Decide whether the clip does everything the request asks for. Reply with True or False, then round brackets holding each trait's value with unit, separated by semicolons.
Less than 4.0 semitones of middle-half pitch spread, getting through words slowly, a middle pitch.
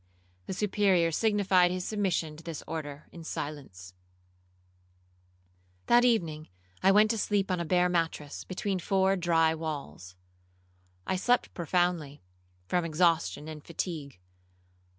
True (3.6 semitones; 125 wpm; 170 Hz)